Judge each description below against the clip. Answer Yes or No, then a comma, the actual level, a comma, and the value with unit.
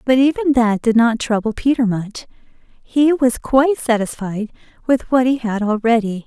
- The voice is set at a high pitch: Yes, high, 240 Hz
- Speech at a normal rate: Yes, average, 165 wpm